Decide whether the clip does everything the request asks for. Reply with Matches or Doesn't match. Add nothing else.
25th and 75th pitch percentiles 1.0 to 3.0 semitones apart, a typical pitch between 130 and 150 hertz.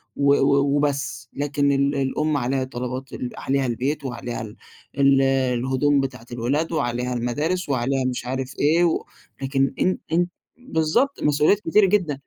Matches